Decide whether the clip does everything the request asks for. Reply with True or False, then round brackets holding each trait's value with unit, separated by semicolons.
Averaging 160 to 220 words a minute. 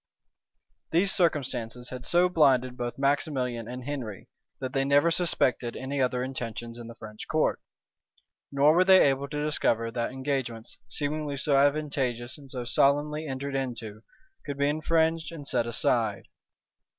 False (150 wpm)